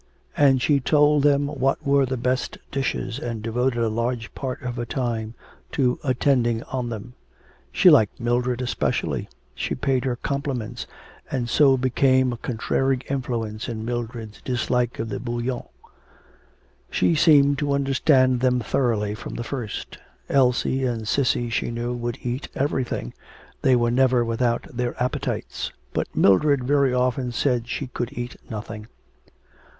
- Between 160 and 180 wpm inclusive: No, average, 145 wpm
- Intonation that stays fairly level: Yes, narrow, 2.1 semitones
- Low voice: Yes, low, 125 Hz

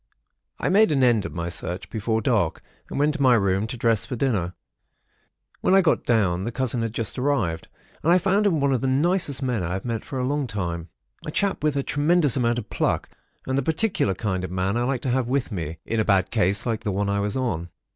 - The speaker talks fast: Yes, fast, 245 wpm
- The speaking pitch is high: No, low, 120 Hz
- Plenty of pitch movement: Yes, wide, 5.9 semitones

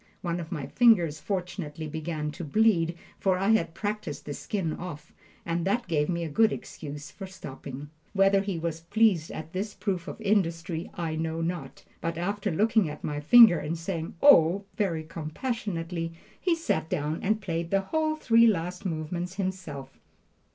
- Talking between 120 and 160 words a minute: No, average, 170 wpm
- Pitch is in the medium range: Yes, medium, 170 Hz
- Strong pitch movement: No, average, 3.9 semitones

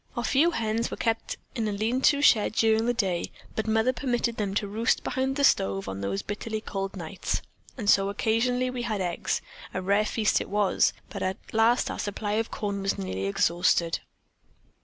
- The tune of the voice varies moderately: Yes, average, 3.1 semitones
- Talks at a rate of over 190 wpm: Yes, average, 200 wpm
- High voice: Yes, high, 215 Hz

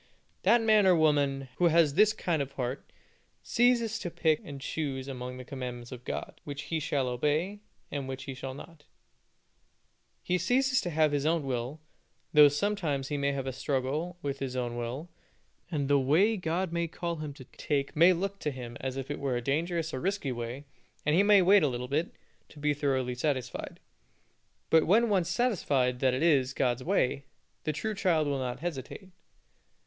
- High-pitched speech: No, medium, 145 Hz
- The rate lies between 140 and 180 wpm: No, average, 195 wpm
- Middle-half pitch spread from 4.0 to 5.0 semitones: Yes, average, 4.6 semitones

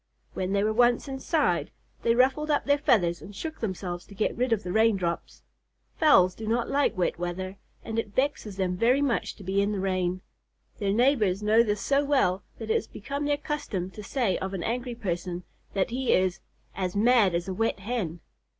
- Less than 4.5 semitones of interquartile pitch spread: No, average, 5.0 semitones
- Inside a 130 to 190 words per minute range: No, fast, 205 wpm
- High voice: Yes, high, 210 Hz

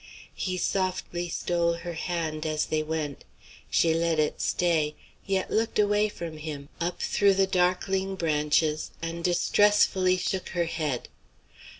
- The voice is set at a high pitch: No, medium, 170 Hz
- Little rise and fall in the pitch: No, average, 3.0 semitones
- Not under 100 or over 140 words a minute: Yes, slow, 135 wpm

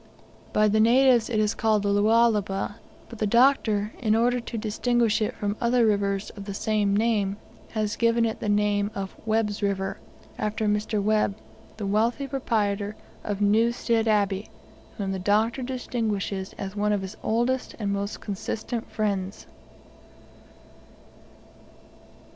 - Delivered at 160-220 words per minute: No, average, 140 wpm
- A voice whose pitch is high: Yes, high, 215 Hz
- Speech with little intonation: Yes, narrow, 2.2 semitones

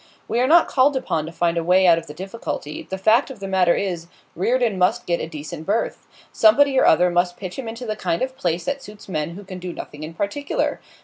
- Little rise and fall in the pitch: No, wide, 5.4 semitones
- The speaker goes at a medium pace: No, fast, 245 wpm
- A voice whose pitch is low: No, high, 190 Hz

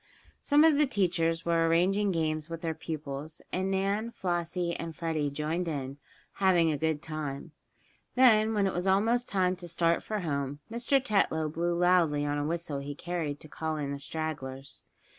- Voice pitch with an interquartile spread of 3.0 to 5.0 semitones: Yes, average, 3.7 semitones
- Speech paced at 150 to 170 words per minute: No, average, 180 wpm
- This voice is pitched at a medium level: Yes, medium, 165 Hz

